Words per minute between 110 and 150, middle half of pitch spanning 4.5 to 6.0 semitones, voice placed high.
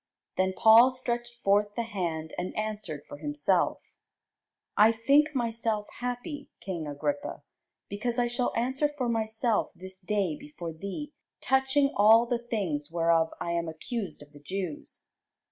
Yes: average, 145 wpm; wide, 5.4 semitones; high, 220 Hz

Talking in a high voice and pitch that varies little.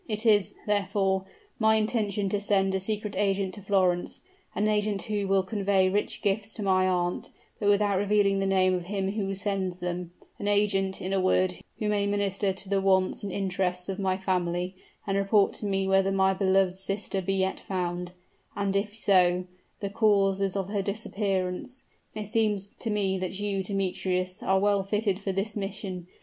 Yes: high, 195 Hz; narrow, 1.4 semitones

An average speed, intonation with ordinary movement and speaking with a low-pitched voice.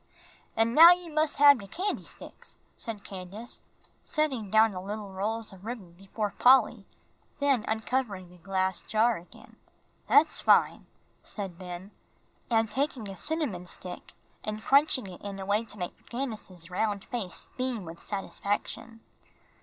No: average, 145 wpm; average, 4.5 semitones; high, 215 Hz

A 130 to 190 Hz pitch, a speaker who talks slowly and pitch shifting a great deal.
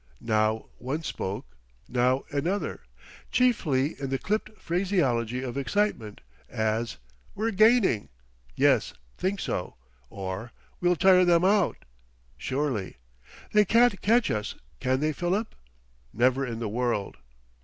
Yes: medium, 140 Hz; slow, 120 wpm; wide, 8.7 semitones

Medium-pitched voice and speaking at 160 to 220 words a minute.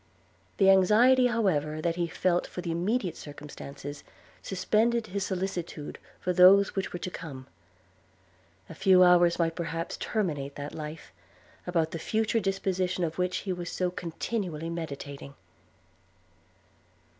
No: medium, 180 Hz; slow, 135 wpm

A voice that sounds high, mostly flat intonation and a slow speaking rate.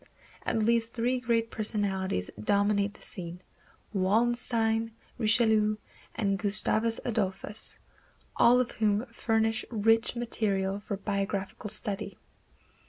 Yes: high, 215 Hz; narrow, 2.2 semitones; slow, 100 wpm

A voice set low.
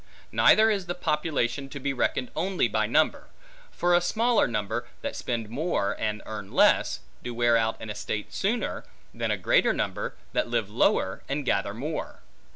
Yes: low, 125 Hz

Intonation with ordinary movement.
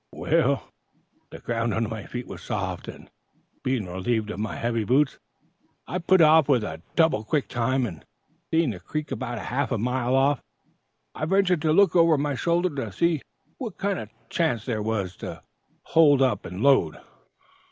No: wide, 6.2 semitones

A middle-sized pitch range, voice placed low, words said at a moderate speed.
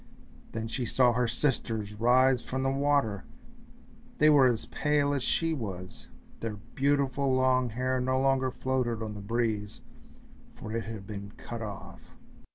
Yes: average, 3.3 semitones; low, 125 Hz; average, 155 wpm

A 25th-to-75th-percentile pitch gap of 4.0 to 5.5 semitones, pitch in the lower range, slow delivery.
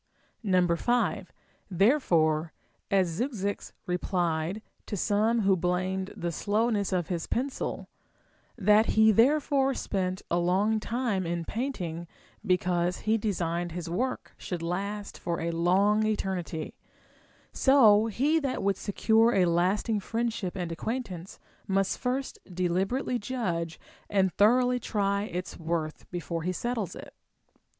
No: average, 4.3 semitones; high, 195 Hz; slow, 125 wpm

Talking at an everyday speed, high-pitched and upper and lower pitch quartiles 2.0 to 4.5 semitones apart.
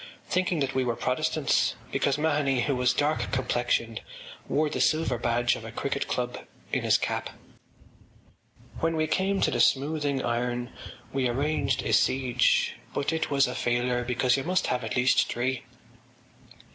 No: average, 165 wpm; low, 130 Hz; average, 3.3 semitones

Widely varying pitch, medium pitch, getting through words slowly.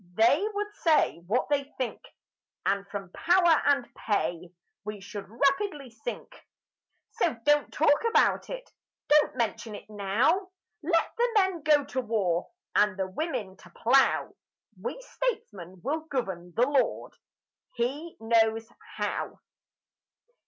No: wide, 7.4 semitones; very high, 250 Hz; slow, 130 wpm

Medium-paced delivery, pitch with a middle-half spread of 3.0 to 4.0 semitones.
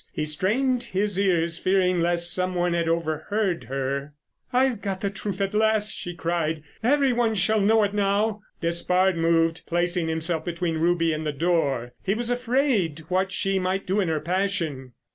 Yes: average, 175 wpm; average, 3.7 semitones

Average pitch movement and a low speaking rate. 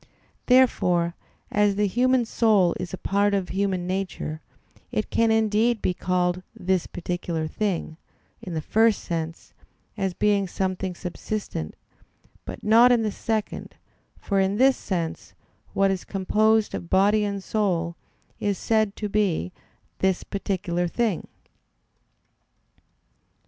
Yes: average, 3.2 semitones; slow, 130 wpm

